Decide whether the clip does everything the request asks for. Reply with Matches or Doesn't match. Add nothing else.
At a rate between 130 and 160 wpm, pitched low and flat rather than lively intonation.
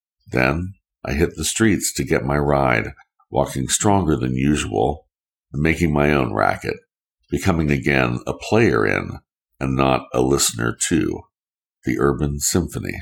Doesn't match